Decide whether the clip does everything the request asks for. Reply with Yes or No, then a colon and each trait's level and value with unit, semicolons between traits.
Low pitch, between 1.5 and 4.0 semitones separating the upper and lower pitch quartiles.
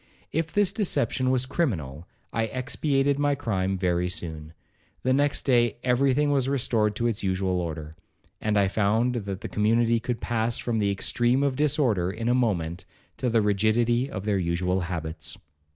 No: low, 115 Hz; wide, 5.5 semitones